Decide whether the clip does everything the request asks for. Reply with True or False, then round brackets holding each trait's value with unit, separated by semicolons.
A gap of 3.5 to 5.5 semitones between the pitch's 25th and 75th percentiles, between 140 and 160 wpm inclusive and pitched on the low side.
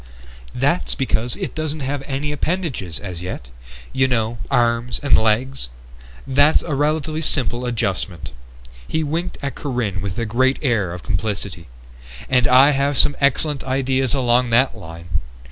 True (4.6 semitones; 145 wpm; 130 Hz)